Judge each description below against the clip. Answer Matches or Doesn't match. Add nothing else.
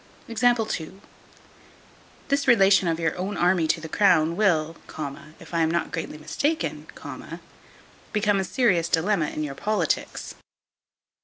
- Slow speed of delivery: Matches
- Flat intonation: Doesn't match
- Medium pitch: Matches